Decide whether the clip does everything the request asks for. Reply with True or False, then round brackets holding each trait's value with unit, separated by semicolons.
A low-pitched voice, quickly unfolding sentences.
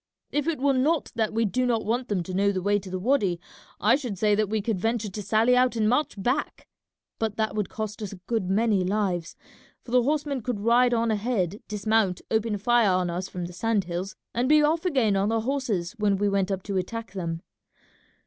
False (215 Hz; 225 wpm)